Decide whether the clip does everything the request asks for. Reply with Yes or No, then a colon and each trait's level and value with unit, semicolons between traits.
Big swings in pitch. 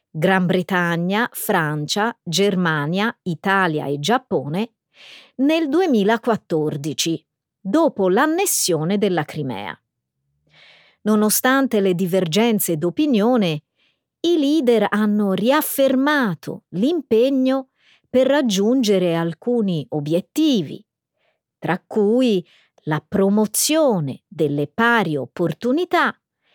Yes: wide, 6.9 semitones